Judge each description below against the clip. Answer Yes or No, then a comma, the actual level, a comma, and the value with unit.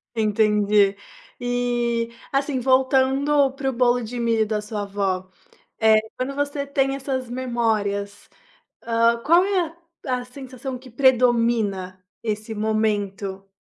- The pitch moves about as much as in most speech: Yes, average, 3.6 semitones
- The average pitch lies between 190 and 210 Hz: No, high, 235 Hz